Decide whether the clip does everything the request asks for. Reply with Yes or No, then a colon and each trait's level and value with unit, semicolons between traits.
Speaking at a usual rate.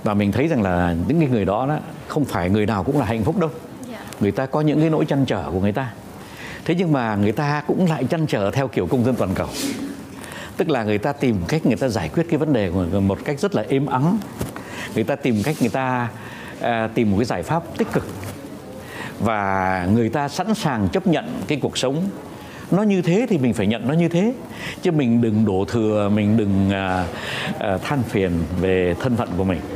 Yes: average, 230 wpm